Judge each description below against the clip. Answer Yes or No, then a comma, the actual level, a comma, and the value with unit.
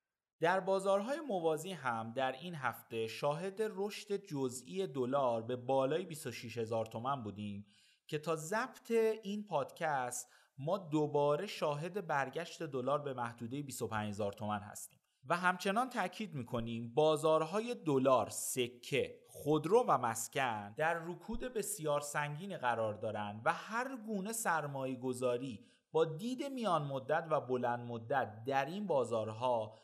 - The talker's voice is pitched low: No, medium, 150 Hz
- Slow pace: No, average, 130 wpm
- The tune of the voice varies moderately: No, wide, 7.9 semitones